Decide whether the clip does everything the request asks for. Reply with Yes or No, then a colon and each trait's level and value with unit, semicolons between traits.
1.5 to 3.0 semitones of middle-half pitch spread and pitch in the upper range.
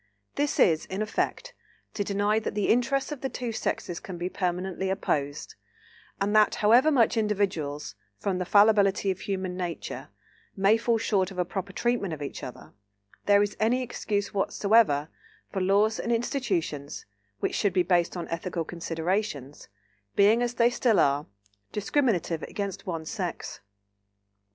No: average, 3.9 semitones; high, 200 Hz